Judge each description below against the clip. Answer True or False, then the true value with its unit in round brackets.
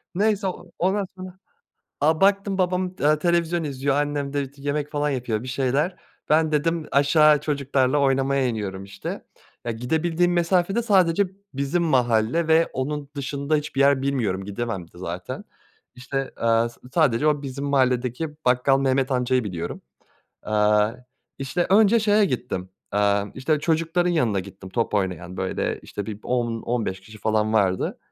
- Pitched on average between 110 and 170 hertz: True (140 Hz)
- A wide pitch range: True (5.8 semitones)